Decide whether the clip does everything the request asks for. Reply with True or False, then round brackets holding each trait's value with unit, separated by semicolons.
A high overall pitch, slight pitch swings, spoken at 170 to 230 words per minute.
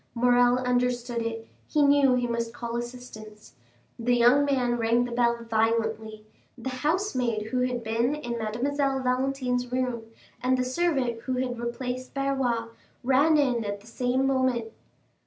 False (245 Hz; 1.8 semitones; 150 wpm)